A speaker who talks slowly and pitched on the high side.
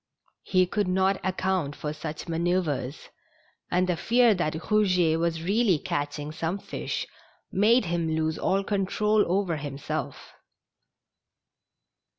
No: slow, 115 wpm; medium, 180 Hz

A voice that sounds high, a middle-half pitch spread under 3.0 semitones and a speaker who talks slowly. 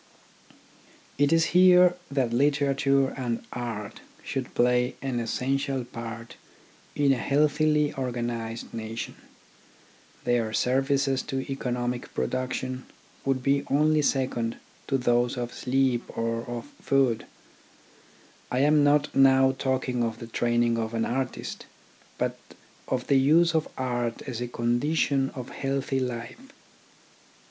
No: low, 130 Hz; narrow, 2.4 semitones; slow, 120 wpm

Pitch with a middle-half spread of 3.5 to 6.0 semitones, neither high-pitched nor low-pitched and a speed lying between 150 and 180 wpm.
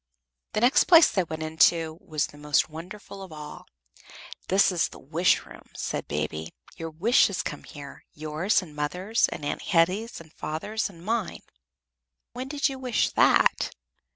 Yes: average, 5.3 semitones; medium, 170 Hz; average, 160 wpm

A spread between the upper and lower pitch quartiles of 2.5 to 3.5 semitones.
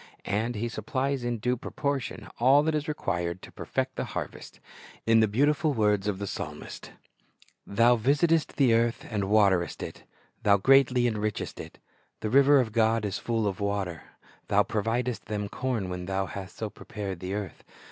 No: average, 3.9 semitones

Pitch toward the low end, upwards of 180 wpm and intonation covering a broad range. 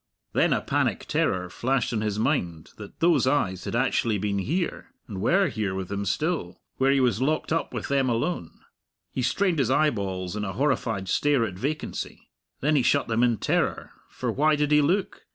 Yes: low, 125 Hz; average, 195 wpm; wide, 6.8 semitones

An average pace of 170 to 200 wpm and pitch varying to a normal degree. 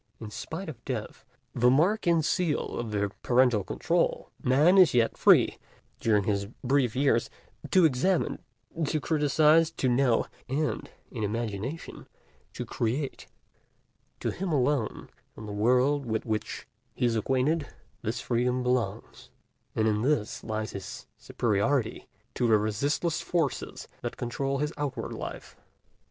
No: average, 140 wpm; average, 4.9 semitones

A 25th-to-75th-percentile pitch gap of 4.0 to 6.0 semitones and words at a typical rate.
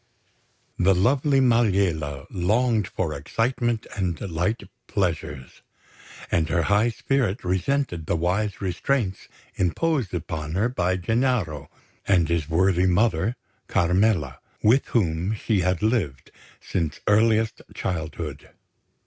No: average, 5.1 semitones; slow, 110 wpm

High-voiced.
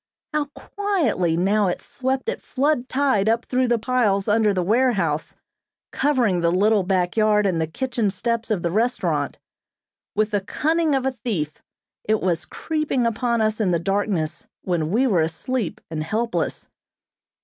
Yes: high, 215 Hz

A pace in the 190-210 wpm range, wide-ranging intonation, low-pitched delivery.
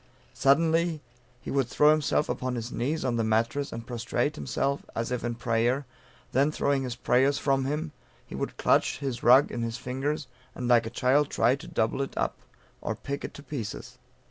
No: average, 195 wpm; average, 3.2 semitones; low, 130 Hz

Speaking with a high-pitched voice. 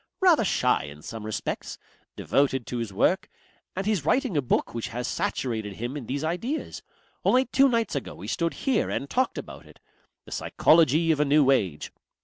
No: medium, 145 Hz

